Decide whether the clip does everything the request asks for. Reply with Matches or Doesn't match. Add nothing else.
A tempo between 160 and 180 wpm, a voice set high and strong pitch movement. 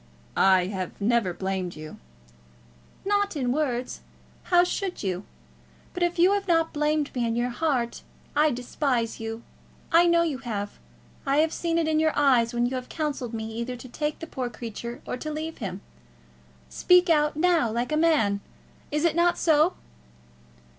Matches